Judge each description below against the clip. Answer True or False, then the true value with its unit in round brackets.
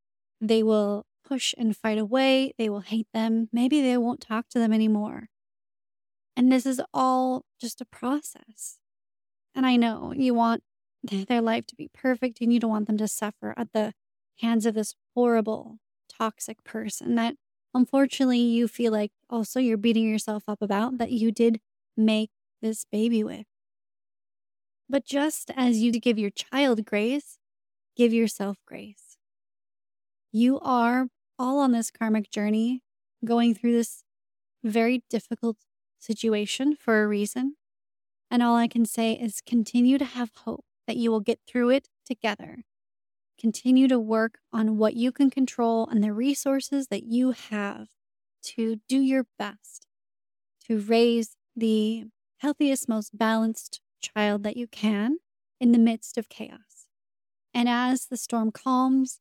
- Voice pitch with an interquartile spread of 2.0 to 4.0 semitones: True (2.8 semitones)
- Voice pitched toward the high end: True (230 Hz)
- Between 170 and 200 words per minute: False (150 wpm)